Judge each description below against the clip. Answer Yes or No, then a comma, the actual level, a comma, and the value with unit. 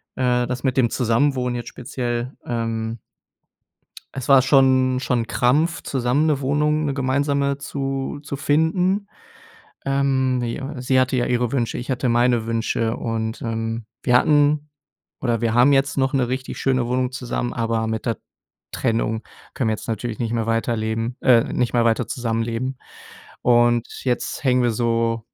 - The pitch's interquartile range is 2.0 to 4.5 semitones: Yes, average, 2.7 semitones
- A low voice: Yes, low, 125 Hz